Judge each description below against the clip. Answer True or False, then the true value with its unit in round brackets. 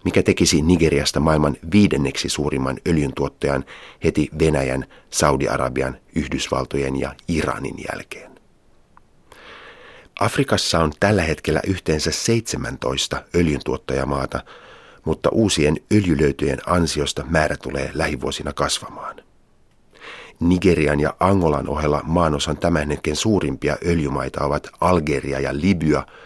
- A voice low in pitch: True (75 Hz)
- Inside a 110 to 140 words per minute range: False (95 wpm)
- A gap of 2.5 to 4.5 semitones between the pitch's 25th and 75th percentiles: True (3.2 semitones)